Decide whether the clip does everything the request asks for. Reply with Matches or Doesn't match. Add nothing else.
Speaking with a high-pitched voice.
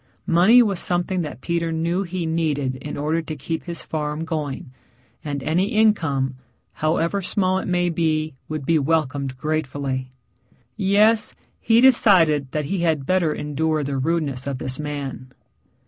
Doesn't match